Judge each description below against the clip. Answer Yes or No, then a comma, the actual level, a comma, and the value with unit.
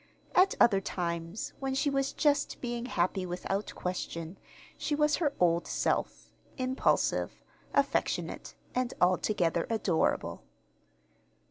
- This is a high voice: Yes, high, 210 Hz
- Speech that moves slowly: Yes, slow, 110 wpm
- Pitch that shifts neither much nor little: No, wide, 7.2 semitones